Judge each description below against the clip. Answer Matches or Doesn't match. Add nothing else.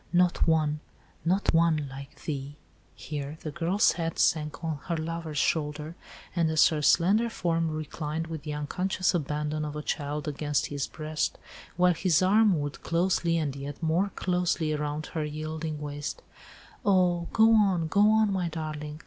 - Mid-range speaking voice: Matches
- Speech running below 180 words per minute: Matches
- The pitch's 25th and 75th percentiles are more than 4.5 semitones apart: Doesn't match